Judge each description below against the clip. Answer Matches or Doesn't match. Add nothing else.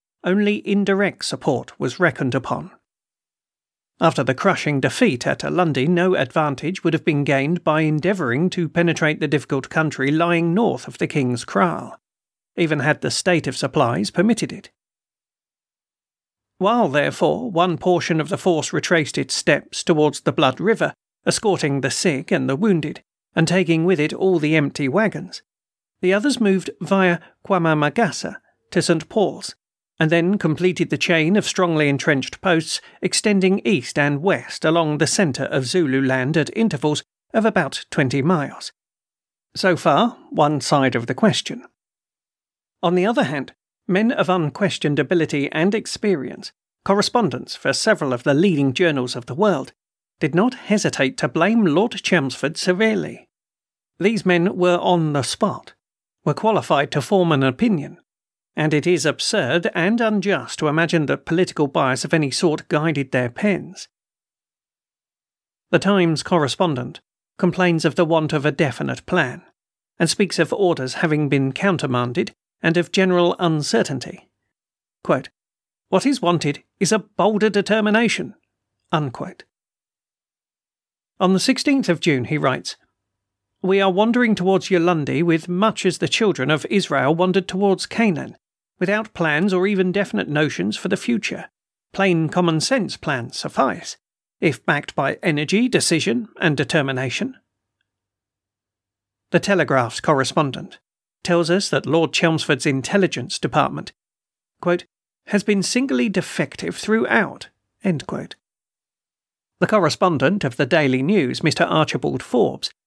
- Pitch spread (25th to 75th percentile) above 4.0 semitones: Matches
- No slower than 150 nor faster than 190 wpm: Doesn't match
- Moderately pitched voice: Matches